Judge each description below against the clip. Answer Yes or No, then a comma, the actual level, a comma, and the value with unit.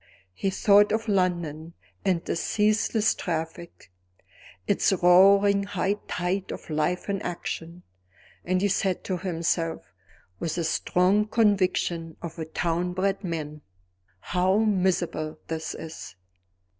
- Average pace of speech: No, slow, 120 wpm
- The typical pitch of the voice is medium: Yes, medium, 180 Hz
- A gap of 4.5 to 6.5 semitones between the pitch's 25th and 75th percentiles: No, average, 3.1 semitones